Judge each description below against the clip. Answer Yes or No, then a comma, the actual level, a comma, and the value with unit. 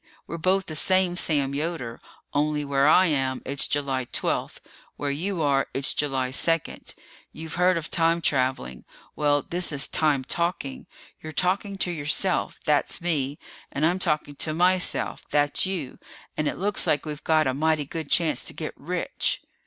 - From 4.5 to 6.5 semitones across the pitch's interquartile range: No, average, 3.5 semitones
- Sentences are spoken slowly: No, average, 170 wpm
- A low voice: No, medium, 155 Hz